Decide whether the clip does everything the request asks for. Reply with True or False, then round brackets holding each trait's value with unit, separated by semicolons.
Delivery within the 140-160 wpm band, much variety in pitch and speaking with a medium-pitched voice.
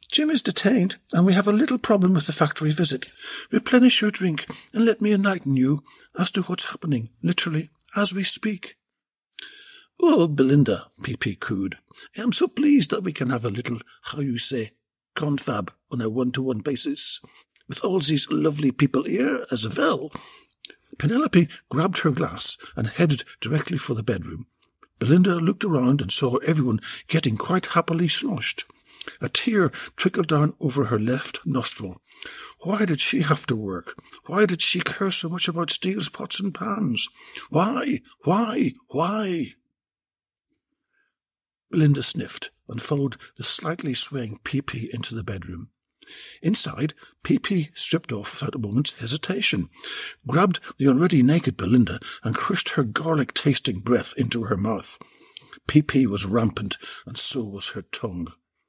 True (155 wpm; 6.9 semitones; 150 Hz)